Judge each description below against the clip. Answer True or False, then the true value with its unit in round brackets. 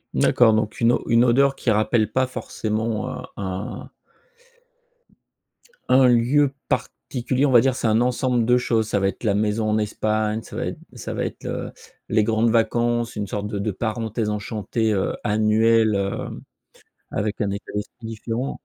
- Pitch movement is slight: True (2.1 semitones)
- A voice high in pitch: False (110 Hz)